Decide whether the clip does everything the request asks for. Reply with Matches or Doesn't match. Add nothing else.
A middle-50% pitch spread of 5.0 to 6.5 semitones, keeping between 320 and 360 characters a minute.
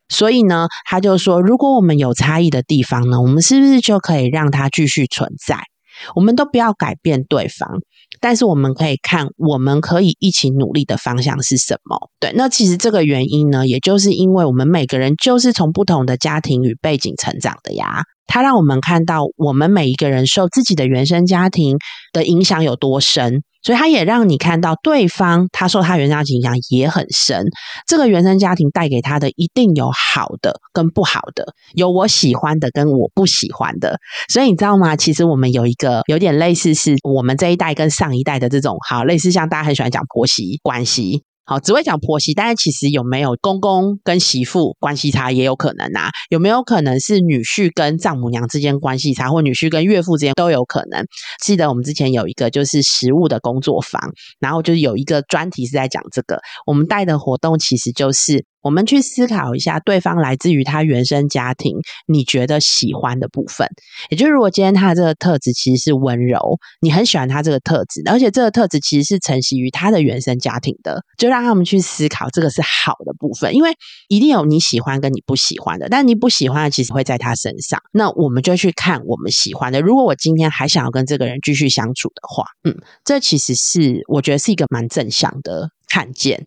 Matches